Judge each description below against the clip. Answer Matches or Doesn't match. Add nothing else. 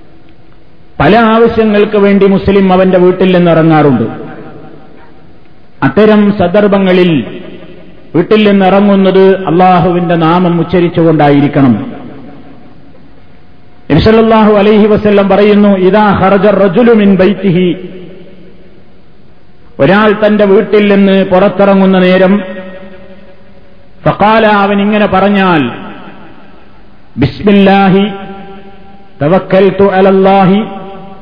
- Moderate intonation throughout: Doesn't match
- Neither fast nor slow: Matches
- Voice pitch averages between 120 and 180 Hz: Doesn't match